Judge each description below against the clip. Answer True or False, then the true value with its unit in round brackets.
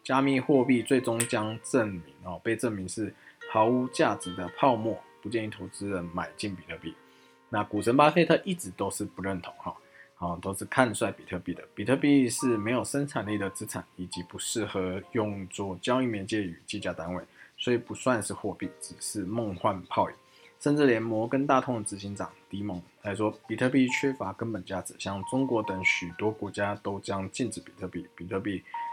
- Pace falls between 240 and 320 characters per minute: True (285 characters per minute)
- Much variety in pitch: False (4.6 semitones)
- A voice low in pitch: True (105 Hz)